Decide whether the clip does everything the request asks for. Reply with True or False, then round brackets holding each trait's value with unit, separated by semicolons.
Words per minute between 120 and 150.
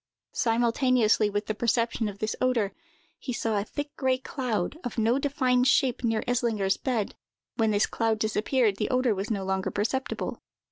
False (170 wpm)